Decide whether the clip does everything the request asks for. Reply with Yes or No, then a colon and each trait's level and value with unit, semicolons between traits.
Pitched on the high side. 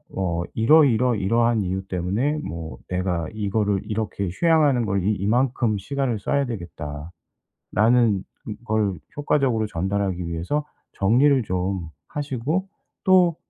No: low, 105 Hz